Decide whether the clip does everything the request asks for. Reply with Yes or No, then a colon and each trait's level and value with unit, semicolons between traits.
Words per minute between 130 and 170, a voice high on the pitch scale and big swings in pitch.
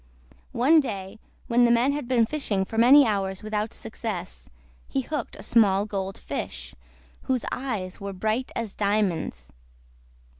No: average, 145 wpm; high, 215 Hz; average, 4.1 semitones